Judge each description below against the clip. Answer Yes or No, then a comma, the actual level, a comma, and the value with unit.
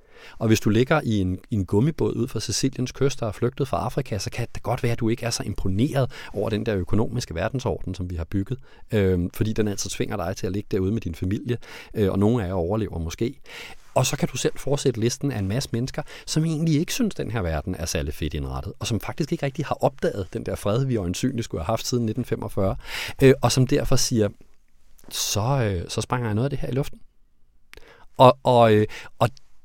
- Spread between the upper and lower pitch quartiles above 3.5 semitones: Yes, average, 4.7 semitones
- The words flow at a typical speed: No, fast, 235 wpm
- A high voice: No, low, 115 Hz